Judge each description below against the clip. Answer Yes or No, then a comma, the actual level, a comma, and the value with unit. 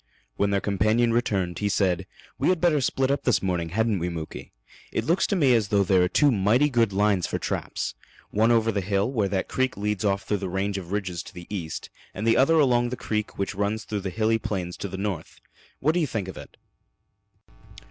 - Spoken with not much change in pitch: No, average, 3.7 semitones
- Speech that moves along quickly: Yes, fast, 230 wpm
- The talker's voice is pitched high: No, low, 105 Hz